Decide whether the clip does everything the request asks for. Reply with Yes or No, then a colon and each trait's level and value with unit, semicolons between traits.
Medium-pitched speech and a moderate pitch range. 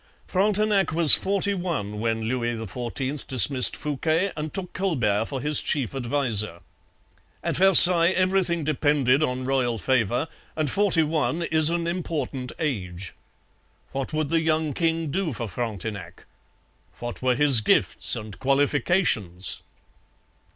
No: medium, 145 Hz; wide, 5.8 semitones